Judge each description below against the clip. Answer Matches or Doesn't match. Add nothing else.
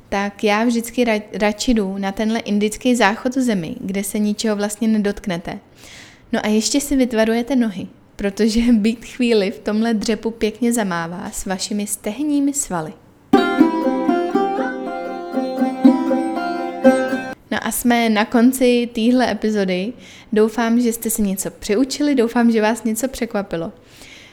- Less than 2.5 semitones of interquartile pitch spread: Doesn't match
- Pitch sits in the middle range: Doesn't match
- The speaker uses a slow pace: Doesn't match